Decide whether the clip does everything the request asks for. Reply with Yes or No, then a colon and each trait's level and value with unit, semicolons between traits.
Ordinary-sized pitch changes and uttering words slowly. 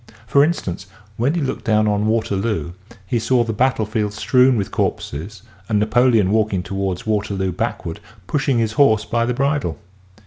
No: average, 3.5 semitones; average, 165 wpm